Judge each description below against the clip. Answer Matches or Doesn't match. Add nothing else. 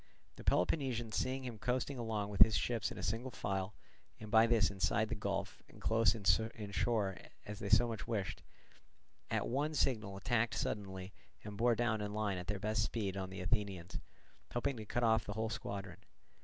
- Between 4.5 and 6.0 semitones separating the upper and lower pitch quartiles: Doesn't match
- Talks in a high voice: Doesn't match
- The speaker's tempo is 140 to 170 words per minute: Doesn't match